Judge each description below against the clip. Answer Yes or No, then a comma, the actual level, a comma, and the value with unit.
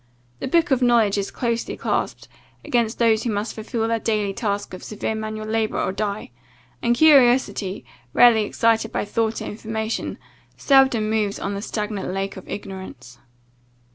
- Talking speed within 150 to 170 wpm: Yes, average, 160 wpm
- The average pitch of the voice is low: No, high, 220 Hz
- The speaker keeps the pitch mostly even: Yes, narrow, 2.3 semitones